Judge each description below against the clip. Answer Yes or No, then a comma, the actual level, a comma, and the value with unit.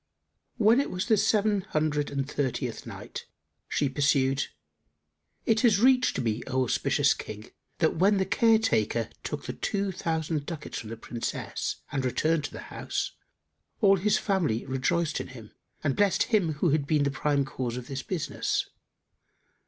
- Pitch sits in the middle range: Yes, medium, 150 Hz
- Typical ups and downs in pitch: No, wide, 6.8 semitones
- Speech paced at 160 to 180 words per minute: Yes, average, 165 wpm